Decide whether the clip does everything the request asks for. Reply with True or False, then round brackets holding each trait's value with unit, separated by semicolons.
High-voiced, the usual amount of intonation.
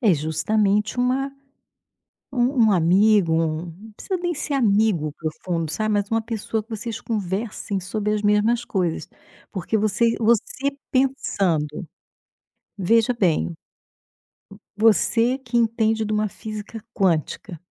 True (215 Hz; 3.9 semitones)